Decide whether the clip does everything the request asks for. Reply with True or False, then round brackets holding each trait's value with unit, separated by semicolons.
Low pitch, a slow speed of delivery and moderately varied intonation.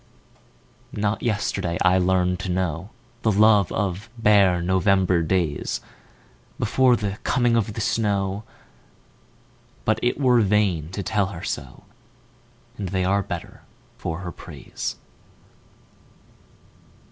True (100 Hz; 100 wpm; 4.0 semitones)